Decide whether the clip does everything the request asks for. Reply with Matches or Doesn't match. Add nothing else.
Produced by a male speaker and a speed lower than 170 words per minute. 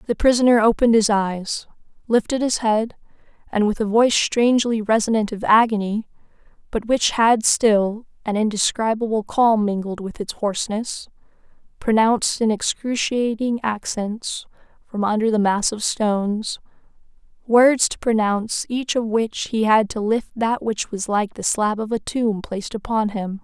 Doesn't match